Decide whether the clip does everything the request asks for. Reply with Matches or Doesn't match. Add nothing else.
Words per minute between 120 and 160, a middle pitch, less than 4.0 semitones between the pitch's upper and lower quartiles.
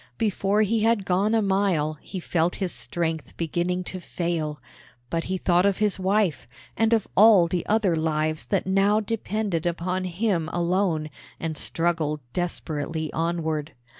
Matches